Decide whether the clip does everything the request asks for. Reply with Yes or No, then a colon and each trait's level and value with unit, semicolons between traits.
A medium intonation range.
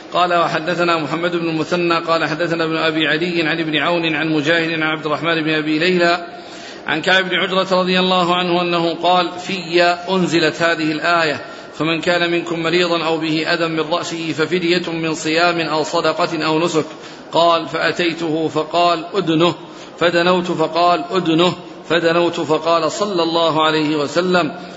No: narrow, 1.6 semitones